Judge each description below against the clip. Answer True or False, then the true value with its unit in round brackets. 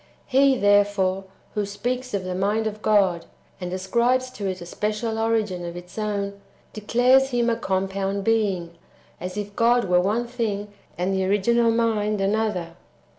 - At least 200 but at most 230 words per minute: False (165 wpm)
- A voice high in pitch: True (205 Hz)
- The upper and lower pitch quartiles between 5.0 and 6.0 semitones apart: False (3.2 semitones)